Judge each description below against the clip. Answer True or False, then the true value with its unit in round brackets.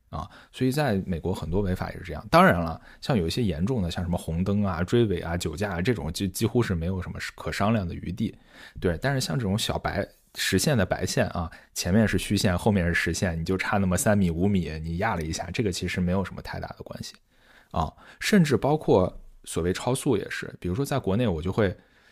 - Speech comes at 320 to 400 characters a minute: True (335 characters per minute)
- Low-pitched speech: True (95 Hz)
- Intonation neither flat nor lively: True (4.1 semitones)